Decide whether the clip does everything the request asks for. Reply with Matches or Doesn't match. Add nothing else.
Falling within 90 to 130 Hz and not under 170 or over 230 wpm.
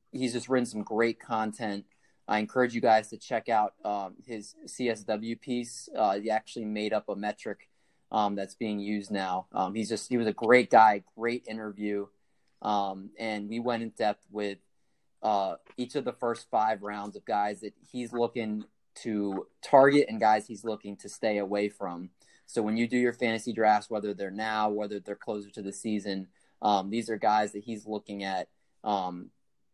Matches